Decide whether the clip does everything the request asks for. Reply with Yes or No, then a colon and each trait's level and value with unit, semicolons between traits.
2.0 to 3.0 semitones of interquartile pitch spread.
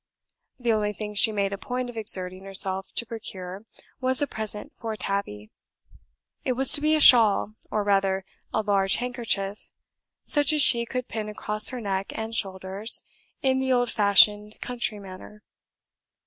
No: average, 3.7 semitones